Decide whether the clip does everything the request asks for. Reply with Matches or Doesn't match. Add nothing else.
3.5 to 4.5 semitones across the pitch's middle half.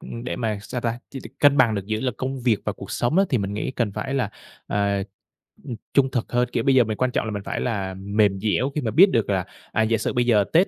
Matches